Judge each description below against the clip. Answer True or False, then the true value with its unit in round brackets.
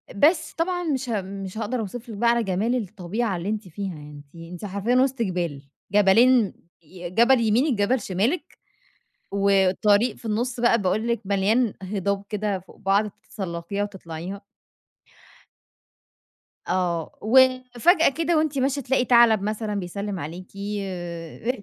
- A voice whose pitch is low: False (210 Hz)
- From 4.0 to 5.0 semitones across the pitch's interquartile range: True (4.3 semitones)